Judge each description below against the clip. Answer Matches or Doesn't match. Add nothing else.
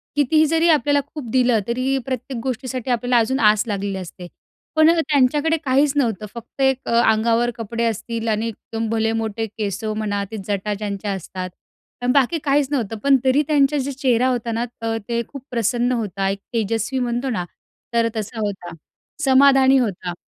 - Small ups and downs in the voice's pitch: Doesn't match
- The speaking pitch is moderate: Doesn't match